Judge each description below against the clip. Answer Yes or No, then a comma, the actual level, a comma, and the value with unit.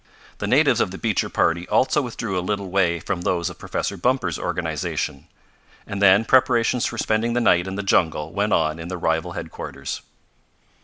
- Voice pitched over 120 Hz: No, very low, 95 Hz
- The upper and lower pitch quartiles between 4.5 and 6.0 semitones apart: Yes, average, 4.8 semitones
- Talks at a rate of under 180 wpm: No, average, 185 wpm